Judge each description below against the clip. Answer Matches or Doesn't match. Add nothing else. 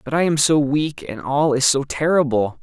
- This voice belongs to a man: Matches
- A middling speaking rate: Doesn't match